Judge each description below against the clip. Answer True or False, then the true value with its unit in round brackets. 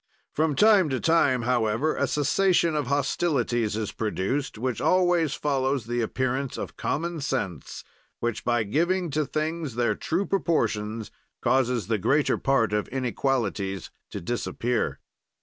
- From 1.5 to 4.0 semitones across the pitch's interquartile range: False (5.1 semitones)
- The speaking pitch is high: False (130 Hz)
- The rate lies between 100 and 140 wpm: True (135 wpm)